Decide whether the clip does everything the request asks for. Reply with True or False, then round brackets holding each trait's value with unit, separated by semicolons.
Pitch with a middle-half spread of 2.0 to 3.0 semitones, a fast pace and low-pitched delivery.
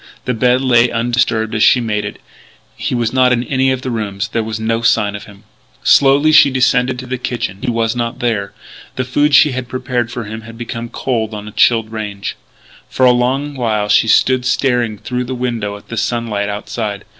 True (2.5 semitones; 215 wpm; 120 Hz)